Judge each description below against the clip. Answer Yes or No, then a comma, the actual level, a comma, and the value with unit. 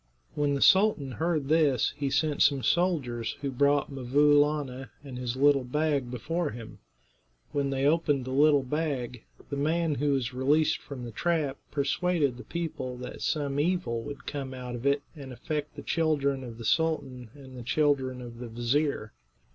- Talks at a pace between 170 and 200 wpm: Yes, average, 175 wpm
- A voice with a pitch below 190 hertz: Yes, medium, 140 Hz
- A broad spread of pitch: No, average, 3.0 semitones